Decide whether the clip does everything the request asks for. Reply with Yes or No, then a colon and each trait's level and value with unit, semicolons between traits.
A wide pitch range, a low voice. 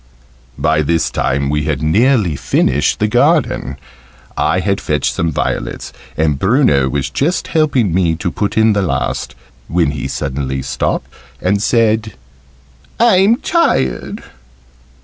Yes: wide, 8.3 semitones; very low, 90 Hz